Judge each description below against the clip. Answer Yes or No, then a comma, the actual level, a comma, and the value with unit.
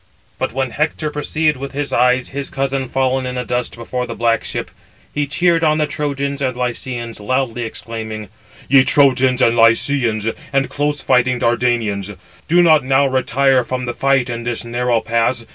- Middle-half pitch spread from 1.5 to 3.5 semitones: Yes, average, 2.8 semitones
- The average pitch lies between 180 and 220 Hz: No, low, 130 Hz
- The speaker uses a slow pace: No, average, 175 wpm